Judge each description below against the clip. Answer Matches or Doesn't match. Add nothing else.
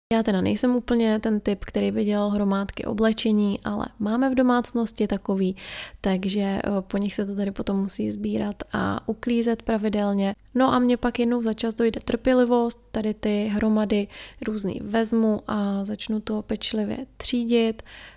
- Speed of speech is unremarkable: Matches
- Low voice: Doesn't match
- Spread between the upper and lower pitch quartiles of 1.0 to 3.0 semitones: Matches